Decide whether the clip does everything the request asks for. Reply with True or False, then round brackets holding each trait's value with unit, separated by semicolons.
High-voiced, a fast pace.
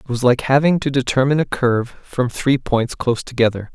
False (130 Hz; 210 wpm)